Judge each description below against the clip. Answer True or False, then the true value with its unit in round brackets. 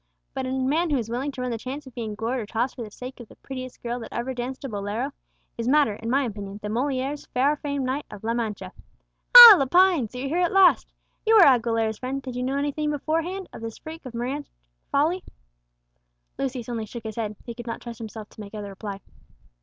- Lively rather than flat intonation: False (3.8 semitones)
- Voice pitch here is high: True (255 Hz)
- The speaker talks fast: True (230 wpm)